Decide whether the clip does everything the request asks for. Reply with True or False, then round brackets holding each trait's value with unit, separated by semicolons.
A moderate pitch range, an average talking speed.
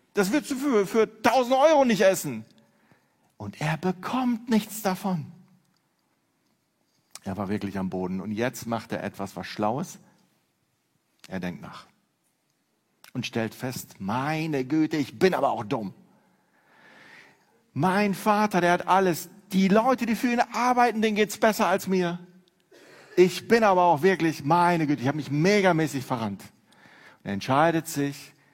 False (6.8 semitones; 145 wpm)